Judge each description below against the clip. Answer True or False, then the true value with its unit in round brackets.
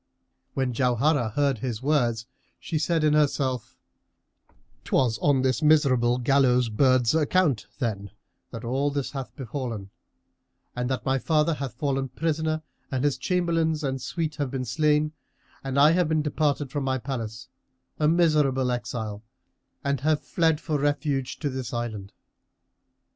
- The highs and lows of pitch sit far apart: False (3.5 semitones)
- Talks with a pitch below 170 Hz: True (135 Hz)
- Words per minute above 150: False (145 wpm)